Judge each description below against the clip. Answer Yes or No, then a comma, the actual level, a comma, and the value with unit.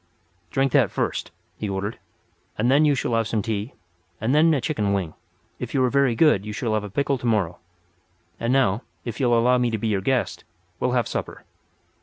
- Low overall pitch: Yes, low, 115 Hz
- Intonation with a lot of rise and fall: No, average, 4.2 semitones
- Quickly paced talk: Yes, fast, 210 wpm